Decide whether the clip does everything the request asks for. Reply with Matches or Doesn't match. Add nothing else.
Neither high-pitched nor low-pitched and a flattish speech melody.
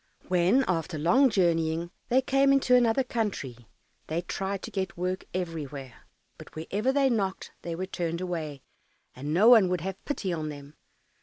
Doesn't match